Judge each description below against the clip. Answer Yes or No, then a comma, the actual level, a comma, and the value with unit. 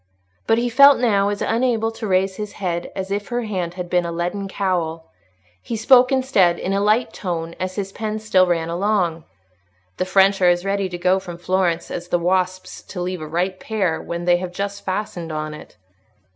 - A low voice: No, medium, 185 Hz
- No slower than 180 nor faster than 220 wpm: Yes, fast, 205 wpm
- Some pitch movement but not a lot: Yes, average, 3.0 semitones